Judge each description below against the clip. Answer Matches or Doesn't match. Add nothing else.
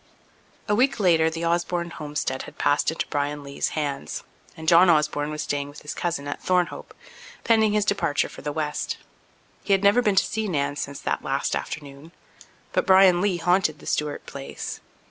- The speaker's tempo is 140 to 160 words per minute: Doesn't match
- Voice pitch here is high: Doesn't match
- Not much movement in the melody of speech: Doesn't match